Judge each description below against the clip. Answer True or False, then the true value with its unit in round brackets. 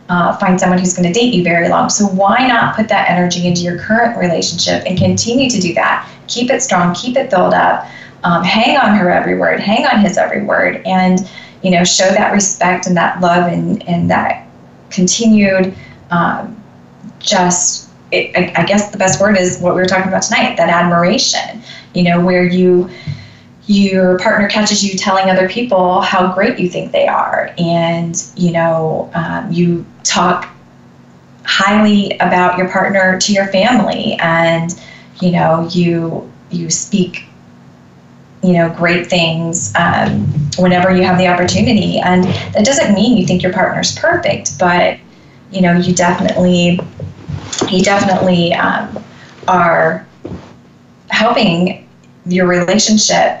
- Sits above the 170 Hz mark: True (185 Hz)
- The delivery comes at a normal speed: True (155 wpm)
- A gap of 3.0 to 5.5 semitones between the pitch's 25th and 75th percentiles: False (2.4 semitones)